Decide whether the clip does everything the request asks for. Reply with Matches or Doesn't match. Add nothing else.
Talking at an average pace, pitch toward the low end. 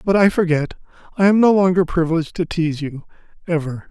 Doesn't match